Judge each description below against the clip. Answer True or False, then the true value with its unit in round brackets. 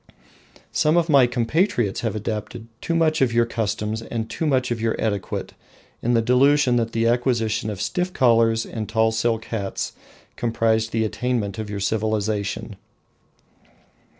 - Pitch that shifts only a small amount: True (2.2 semitones)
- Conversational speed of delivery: True (150 wpm)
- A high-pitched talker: False (115 Hz)